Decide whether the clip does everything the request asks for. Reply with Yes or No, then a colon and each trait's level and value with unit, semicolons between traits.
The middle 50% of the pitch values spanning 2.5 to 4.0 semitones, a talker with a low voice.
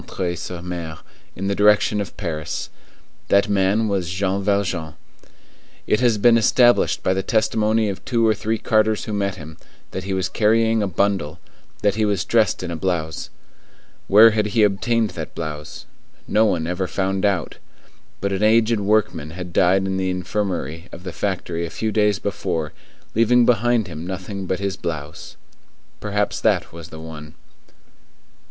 Yes: average, 3.3 semitones; low, 100 Hz